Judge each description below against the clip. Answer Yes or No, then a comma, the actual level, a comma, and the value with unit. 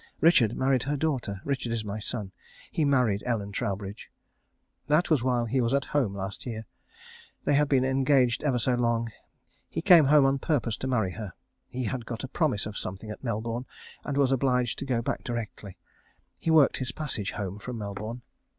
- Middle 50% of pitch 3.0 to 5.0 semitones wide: Yes, average, 4.0 semitones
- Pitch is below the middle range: Yes, low, 125 Hz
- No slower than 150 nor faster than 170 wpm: No, average, 190 wpm